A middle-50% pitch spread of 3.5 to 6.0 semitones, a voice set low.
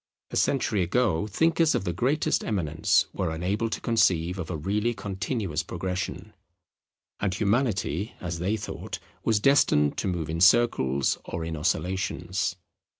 Yes: average, 4.8 semitones; very low, 95 Hz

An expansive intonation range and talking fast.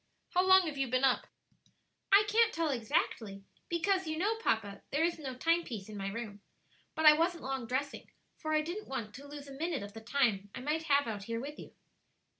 Yes: wide, 6.3 semitones; fast, 220 wpm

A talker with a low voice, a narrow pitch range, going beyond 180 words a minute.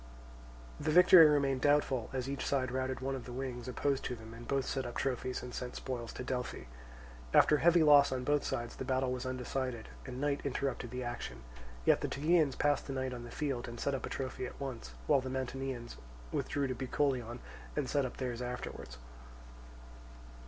Yes: low, 130 Hz; narrow, 2.0 semitones; average, 195 wpm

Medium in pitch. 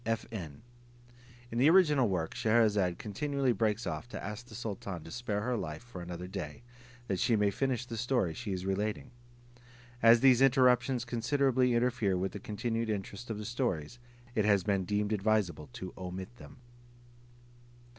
No: low, 110 Hz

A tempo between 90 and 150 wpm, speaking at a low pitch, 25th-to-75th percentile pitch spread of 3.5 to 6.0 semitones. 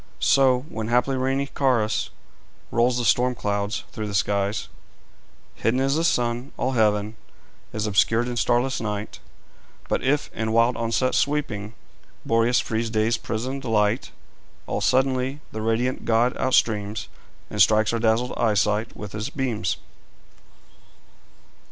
No: slow, 135 wpm; low, 115 Hz; average, 3.0 semitones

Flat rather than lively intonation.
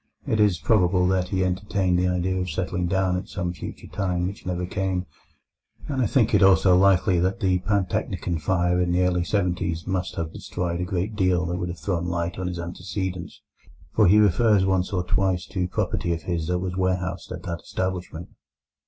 Yes: narrow, 1.3 semitones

